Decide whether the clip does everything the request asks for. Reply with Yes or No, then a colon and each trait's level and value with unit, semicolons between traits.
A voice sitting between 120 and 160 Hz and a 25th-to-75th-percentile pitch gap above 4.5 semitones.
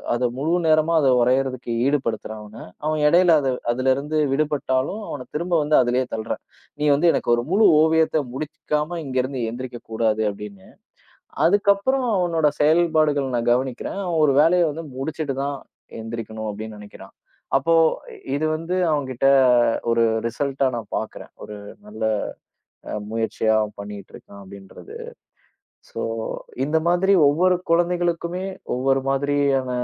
Yes: medium, 140 Hz; average, 5.3 semitones